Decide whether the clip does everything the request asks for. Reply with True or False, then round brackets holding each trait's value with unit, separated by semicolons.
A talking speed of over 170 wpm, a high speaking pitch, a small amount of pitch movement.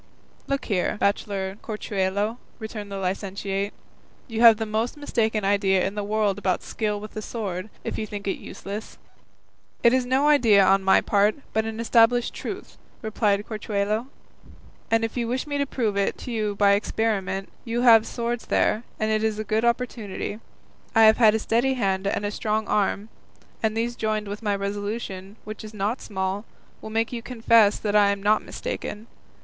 True (180 wpm; 215 Hz; 2.1 semitones)